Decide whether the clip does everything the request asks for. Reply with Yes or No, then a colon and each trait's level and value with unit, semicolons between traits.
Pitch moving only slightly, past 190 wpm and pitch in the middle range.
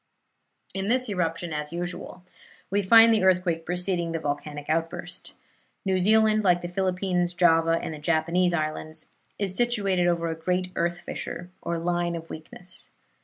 No: narrow, 2.2 semitones; average, 155 wpm; medium, 175 Hz